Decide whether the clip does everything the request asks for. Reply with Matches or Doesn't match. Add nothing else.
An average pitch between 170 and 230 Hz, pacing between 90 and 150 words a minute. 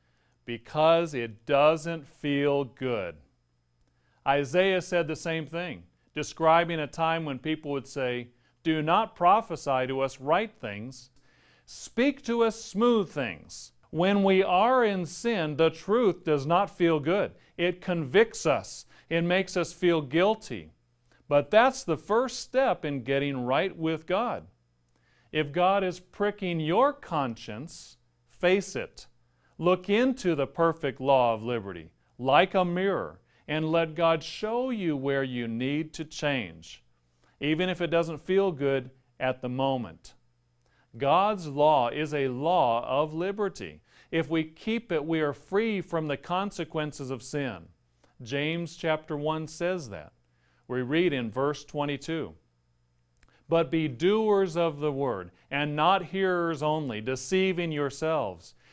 Doesn't match